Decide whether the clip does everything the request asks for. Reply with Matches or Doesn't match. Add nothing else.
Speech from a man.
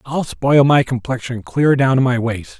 Matches